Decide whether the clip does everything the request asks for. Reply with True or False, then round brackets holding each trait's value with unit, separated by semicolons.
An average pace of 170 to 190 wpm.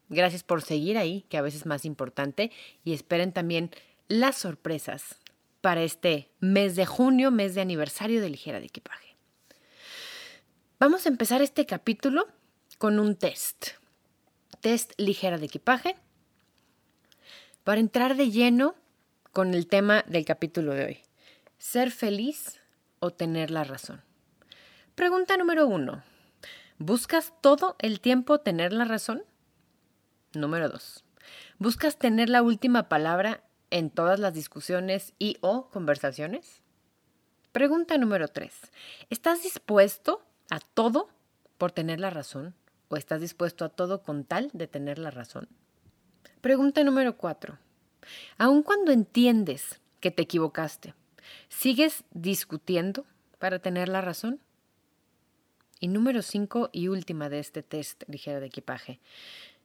False (130 wpm)